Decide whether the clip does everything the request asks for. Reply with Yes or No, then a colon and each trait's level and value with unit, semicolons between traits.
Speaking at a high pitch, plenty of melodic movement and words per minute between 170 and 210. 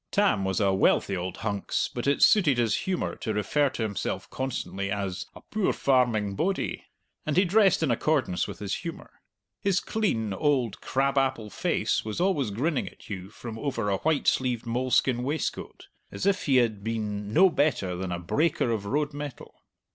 No: low, 125 Hz; wide, 6.4 semitones; average, 180 wpm